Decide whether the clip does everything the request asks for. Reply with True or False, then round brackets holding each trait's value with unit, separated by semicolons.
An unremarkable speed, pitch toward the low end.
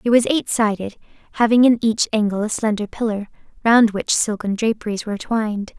False (175 wpm; 220 Hz)